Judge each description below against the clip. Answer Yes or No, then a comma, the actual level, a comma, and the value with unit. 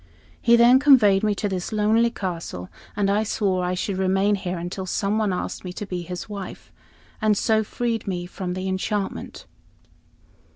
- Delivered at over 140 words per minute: Yes, average, 170 wpm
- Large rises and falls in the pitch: No, average, 2.7 semitones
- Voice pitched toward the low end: No, high, 195 Hz